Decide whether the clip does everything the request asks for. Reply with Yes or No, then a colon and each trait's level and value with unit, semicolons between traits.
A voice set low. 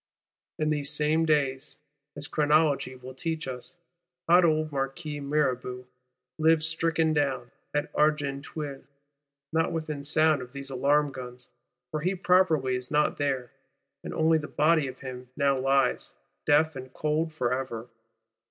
No: medium, 145 Hz